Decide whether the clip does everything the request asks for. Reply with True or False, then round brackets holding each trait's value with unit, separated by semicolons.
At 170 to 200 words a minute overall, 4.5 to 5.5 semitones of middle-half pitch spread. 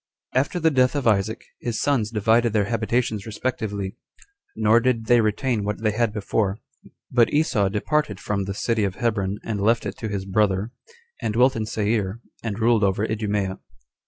False (180 wpm; 2.5 semitones)